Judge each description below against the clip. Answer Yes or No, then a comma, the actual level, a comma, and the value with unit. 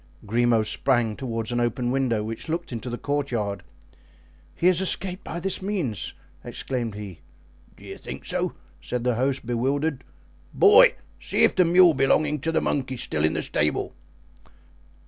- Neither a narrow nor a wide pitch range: No, wide, 5.7 semitones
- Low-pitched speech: Yes, low, 130 Hz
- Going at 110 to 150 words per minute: No, average, 165 wpm